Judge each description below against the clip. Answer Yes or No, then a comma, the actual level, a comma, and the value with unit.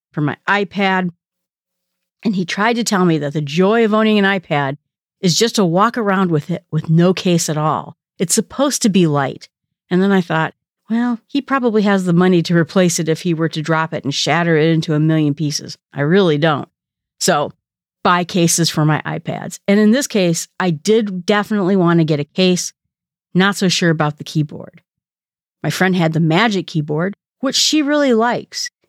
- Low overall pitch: No, medium, 180 Hz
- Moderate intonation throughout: Yes, average, 4.1 semitones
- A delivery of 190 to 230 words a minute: Yes, average, 200 wpm